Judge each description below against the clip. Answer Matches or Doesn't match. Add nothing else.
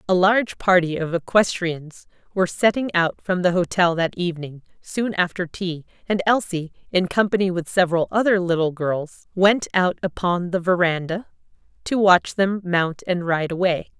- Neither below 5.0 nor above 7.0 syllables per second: Doesn't match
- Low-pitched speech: Doesn't match